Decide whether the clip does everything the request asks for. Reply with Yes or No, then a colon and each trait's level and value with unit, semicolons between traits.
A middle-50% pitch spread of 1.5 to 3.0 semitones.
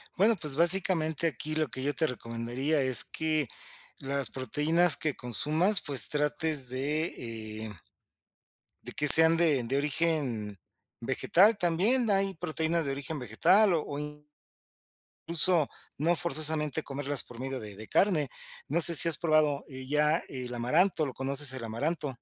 No: average, 3.9 semitones